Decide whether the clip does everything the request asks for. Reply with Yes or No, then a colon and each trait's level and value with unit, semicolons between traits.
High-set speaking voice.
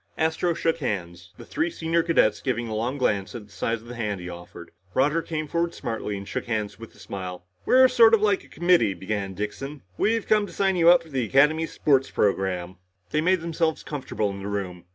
No: low, 130 Hz